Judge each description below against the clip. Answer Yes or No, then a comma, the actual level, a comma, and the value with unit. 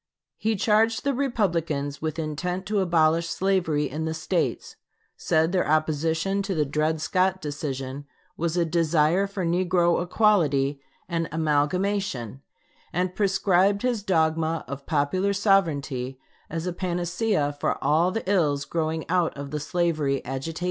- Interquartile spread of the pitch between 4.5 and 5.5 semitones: No, average, 3.9 semitones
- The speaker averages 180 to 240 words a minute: No, average, 140 wpm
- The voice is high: No, medium, 165 Hz